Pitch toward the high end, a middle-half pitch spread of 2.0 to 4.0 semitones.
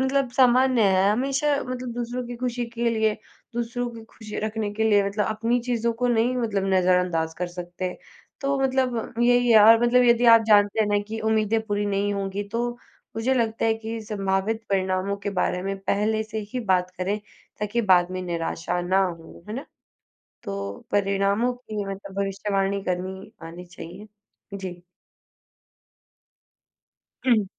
Yes: high, 215 Hz; average, 3.6 semitones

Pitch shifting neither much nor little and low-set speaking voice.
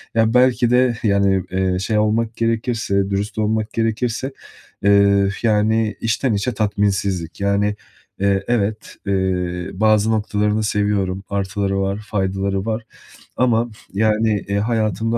No: narrow, 2.2 semitones; low, 105 Hz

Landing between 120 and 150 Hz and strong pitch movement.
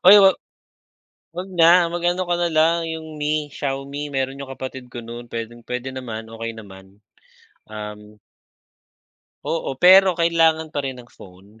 Yes: low, 135 Hz; wide, 6.1 semitones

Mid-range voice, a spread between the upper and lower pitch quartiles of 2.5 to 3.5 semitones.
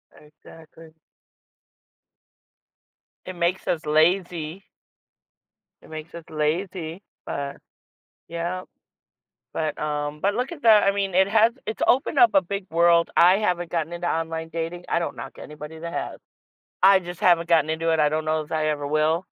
Yes: medium, 170 Hz; average, 2.9 semitones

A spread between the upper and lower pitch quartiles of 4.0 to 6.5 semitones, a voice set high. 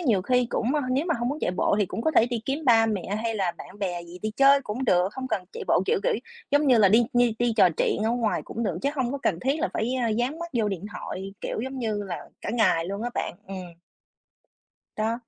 Yes: average, 4.5 semitones; high, 230 Hz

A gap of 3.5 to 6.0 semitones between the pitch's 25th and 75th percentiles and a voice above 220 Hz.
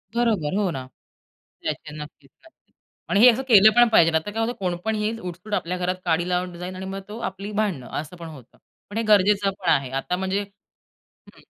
No: average, 4.0 semitones; high, 190 Hz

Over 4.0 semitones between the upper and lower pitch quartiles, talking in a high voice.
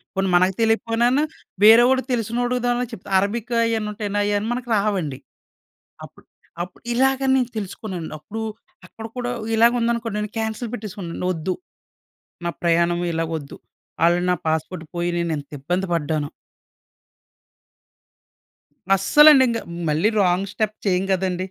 Yes: average, 4.7 semitones; high, 205 Hz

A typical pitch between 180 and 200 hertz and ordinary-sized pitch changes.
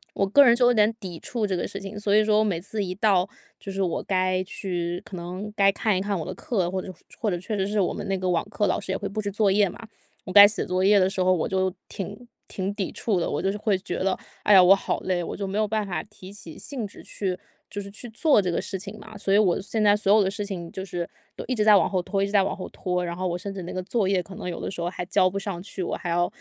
No: high, 195 Hz; narrow, 2.1 semitones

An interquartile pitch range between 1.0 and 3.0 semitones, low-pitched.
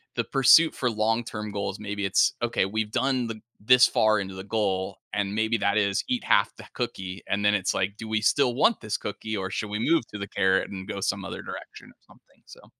Yes: narrow, 2.4 semitones; low, 105 Hz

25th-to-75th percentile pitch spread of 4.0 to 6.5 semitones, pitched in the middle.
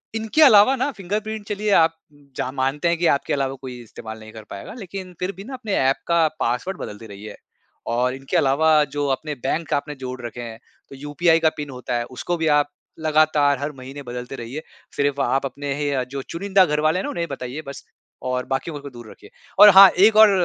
Yes: average, 5.2 semitones; medium, 145 Hz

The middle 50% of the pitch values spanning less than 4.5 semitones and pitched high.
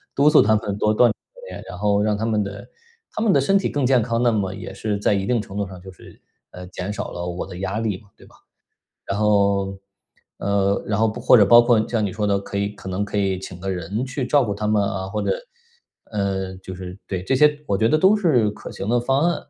No: average, 3.4 semitones; low, 105 Hz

